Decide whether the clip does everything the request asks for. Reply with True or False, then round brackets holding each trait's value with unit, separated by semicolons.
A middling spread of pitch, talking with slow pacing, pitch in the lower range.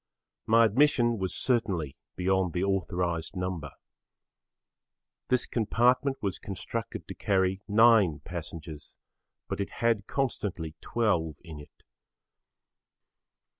True (5.0 semitones; 100 wpm; 95 Hz)